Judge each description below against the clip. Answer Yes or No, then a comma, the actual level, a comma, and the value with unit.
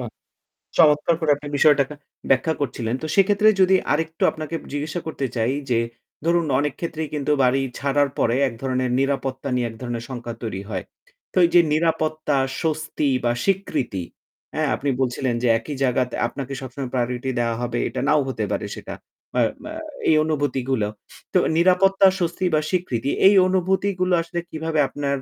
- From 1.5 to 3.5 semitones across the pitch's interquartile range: No, average, 4.4 semitones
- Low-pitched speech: No, medium, 145 Hz